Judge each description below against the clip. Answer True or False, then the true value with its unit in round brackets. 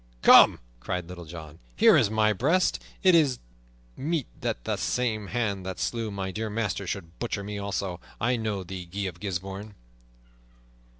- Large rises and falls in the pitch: False (3.6 semitones)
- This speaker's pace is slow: False (165 wpm)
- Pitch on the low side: True (100 Hz)